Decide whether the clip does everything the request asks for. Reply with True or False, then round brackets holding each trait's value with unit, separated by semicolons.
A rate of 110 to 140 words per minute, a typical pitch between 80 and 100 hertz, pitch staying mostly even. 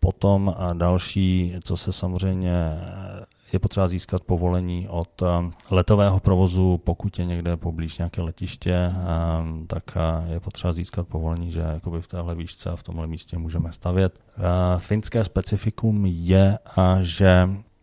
True (130 wpm; 90 Hz; 1.9 semitones)